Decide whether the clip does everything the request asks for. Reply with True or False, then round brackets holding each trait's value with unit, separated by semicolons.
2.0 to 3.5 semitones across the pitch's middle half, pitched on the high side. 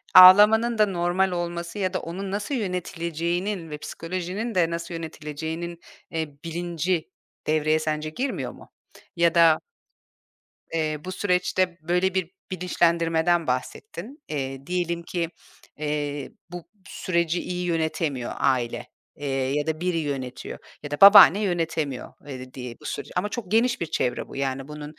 False (3.1 semitones; 170 Hz)